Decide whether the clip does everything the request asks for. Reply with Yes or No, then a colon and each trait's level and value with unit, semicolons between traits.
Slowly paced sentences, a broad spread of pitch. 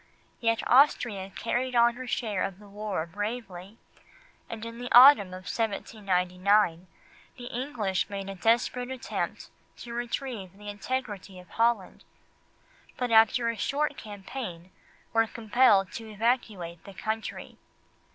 No: slow, 130 wpm; average, 3.7 semitones